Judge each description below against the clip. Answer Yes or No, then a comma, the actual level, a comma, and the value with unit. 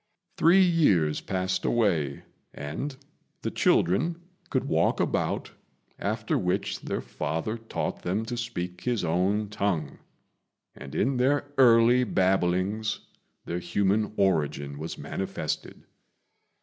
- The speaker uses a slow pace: Yes, slow, 110 wpm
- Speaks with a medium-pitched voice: No, low, 100 Hz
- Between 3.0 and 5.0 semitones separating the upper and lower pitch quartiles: No, wide, 5.4 semitones